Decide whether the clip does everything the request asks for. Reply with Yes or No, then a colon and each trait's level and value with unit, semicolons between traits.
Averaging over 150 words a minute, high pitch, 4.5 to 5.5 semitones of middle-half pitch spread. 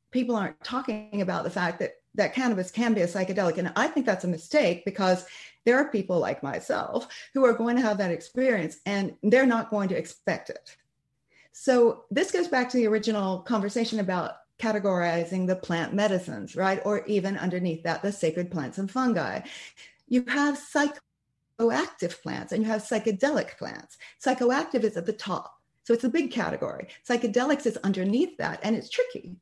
Yes: average, 180 wpm; high, 220 Hz; average, 5.2 semitones